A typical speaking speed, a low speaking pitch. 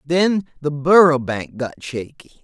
No: average, 150 wpm; medium, 150 Hz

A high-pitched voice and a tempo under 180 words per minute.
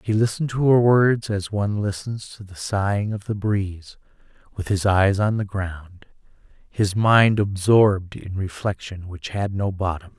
No: low, 100 Hz; average, 170 wpm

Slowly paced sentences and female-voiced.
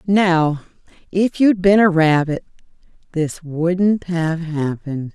Yes: slow, 115 wpm; female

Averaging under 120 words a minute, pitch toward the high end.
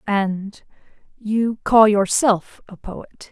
Yes: slow, 90 wpm; high, 210 Hz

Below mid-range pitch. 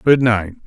Yes: low, 115 Hz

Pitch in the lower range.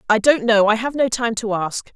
No: high, 225 Hz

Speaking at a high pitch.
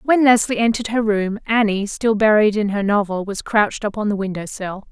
Yes: high, 210 Hz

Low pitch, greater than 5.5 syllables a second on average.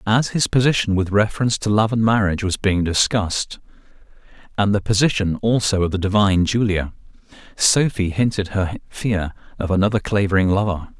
Yes: low, 100 Hz; 5.7 syllables/s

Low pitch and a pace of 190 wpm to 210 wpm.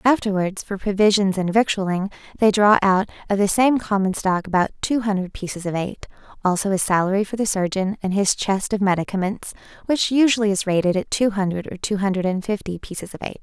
No: high, 200 Hz; average, 200 wpm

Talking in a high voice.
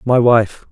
No: low, 115 Hz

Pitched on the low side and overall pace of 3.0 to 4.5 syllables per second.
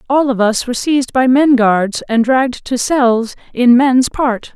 No: very high, 250 Hz; 4.4 syllables/s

